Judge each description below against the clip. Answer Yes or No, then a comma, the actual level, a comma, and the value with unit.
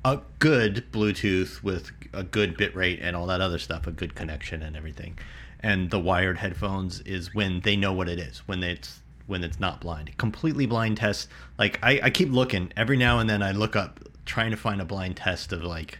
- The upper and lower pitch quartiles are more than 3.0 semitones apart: Yes, average, 3.8 semitones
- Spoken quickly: Yes, fast, 220 wpm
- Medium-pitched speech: No, very low, 95 Hz